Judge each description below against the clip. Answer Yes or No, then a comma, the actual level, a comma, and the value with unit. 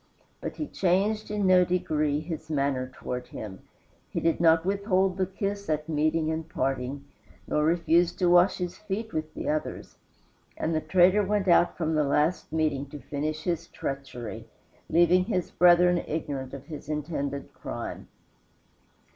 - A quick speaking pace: No, average, 155 wpm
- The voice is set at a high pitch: No, medium, 160 Hz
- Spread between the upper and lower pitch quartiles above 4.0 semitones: No, average, 3.5 semitones